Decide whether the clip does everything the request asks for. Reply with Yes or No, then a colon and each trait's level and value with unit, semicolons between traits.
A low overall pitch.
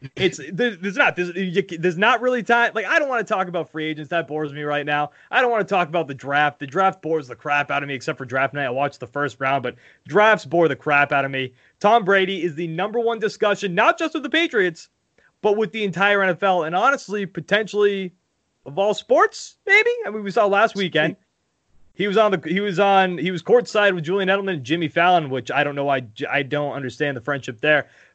No: medium, 180 Hz